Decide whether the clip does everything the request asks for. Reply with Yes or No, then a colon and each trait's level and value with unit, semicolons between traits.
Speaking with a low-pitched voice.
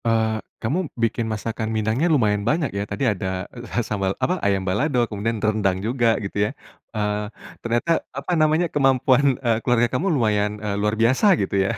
Yes: low, 115 Hz